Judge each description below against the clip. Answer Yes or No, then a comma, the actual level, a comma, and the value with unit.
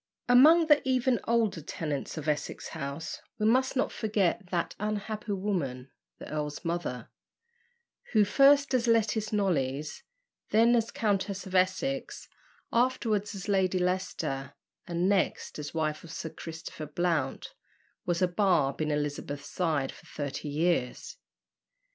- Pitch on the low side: No, medium, 185 Hz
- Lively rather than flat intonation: Yes, wide, 6.2 semitones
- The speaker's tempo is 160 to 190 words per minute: No, slow, 135 wpm